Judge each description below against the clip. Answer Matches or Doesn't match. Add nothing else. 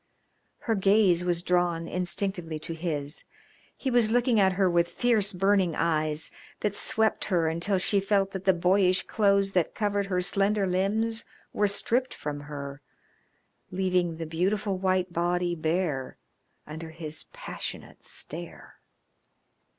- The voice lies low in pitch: Doesn't match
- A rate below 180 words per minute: Matches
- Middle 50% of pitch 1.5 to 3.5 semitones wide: Matches